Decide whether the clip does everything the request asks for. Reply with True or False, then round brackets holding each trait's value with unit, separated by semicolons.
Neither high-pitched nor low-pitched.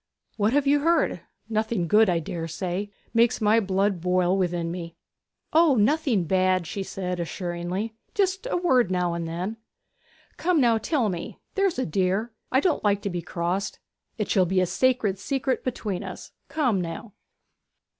False (200 Hz)